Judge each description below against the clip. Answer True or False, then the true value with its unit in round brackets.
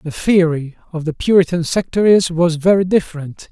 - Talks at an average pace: True (155 wpm)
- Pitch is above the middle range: False (170 Hz)